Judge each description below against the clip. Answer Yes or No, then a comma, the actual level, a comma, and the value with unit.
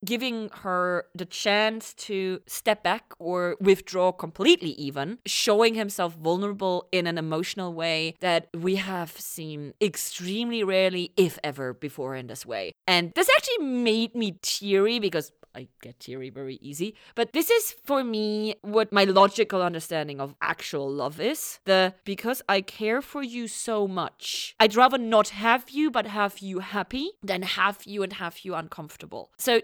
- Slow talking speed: No, average, 160 wpm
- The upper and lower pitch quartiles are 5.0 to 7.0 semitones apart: No, average, 4.4 semitones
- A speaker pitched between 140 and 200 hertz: Yes, high, 190 Hz